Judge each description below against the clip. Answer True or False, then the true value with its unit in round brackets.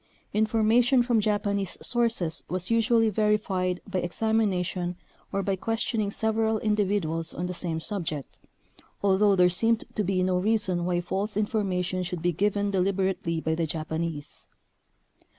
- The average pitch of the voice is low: False (195 Hz)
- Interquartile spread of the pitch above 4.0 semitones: False (3.3 semitones)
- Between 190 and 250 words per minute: False (150 wpm)